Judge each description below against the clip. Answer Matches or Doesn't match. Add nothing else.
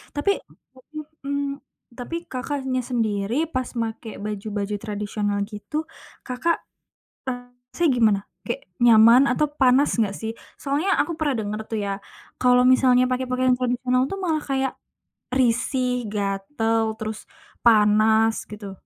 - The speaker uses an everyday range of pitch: Matches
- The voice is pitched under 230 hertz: Doesn't match